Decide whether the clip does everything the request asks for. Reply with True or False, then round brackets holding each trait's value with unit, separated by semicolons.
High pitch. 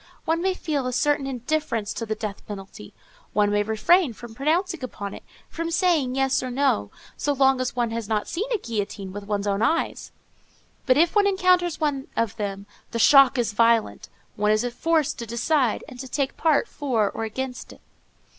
True (255 Hz)